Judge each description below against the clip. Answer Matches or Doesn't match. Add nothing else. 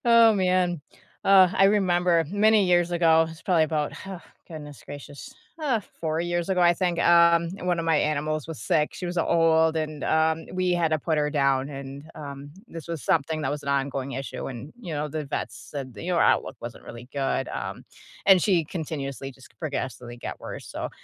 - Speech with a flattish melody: Doesn't match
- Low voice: Doesn't match